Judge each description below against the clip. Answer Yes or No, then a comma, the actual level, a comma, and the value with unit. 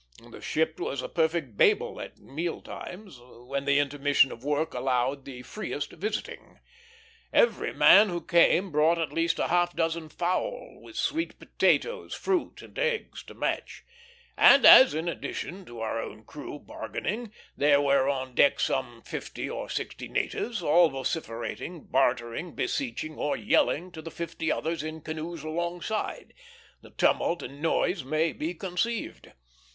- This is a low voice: No, medium, 160 Hz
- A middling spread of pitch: Yes, average, 4.1 semitones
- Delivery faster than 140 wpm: Yes, average, 155 wpm